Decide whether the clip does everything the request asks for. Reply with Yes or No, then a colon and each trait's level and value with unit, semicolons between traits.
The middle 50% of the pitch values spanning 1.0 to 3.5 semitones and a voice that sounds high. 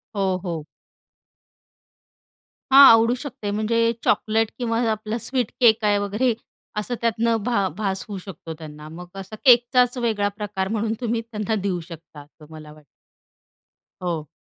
No: average, 4.2 semitones; high, 210 Hz